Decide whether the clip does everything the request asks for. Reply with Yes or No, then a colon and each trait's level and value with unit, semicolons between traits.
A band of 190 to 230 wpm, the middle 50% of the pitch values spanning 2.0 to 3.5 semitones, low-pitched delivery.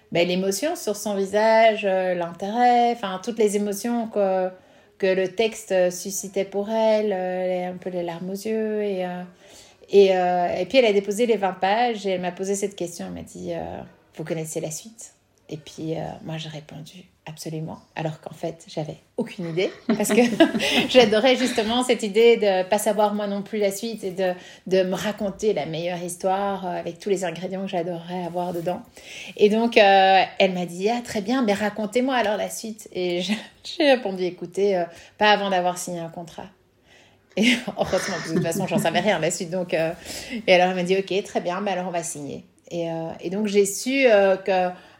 No: average, 205 wpm; average, 3.1 semitones; high, 195 Hz